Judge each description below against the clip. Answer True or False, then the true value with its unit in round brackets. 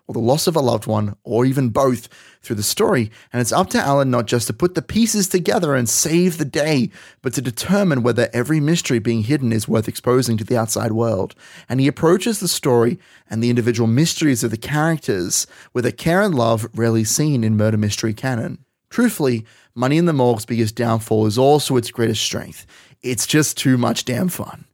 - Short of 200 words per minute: False (205 wpm)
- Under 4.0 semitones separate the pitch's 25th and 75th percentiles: False (4.9 semitones)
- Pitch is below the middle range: True (125 Hz)